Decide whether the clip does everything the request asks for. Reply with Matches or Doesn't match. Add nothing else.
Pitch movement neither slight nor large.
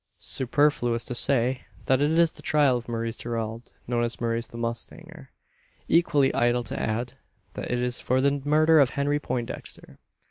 Matches